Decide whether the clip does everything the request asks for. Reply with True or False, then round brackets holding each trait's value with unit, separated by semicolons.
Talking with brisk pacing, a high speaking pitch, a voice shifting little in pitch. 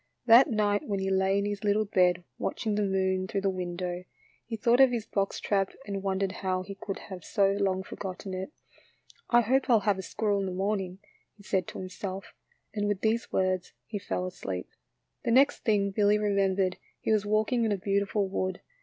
True (210 wpm; 200 Hz; 1.9 semitones)